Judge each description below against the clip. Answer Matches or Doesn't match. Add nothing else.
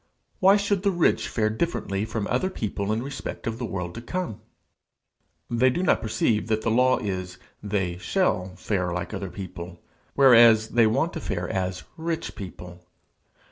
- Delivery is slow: Doesn't match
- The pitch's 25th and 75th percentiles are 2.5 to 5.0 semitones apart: Doesn't match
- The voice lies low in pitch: Matches